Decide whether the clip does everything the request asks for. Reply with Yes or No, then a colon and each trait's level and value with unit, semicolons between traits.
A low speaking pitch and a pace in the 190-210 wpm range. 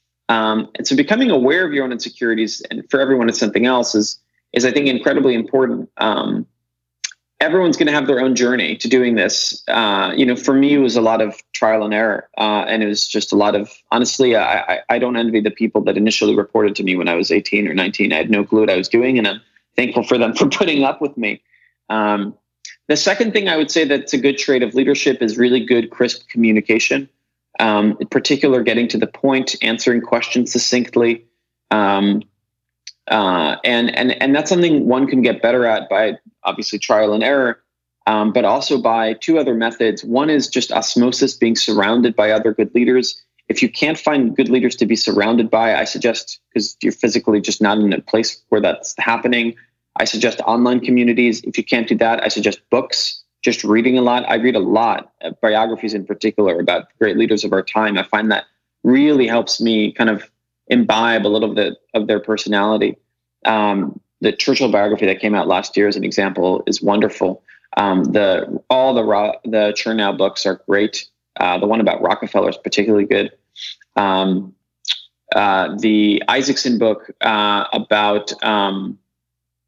Yes: low, 110 Hz; average, 195 wpm